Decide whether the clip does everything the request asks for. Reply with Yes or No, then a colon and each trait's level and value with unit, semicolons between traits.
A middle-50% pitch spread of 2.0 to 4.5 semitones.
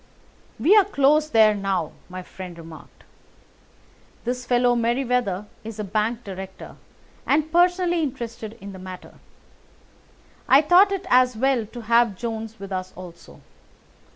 No: wide, 5.4 semitones